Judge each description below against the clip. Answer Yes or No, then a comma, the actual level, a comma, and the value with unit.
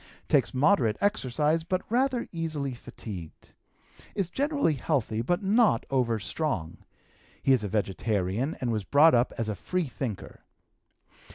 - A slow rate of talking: Yes, slow, 130 wpm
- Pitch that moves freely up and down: Yes, wide, 7.8 semitones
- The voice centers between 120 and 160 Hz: Yes, low, 135 Hz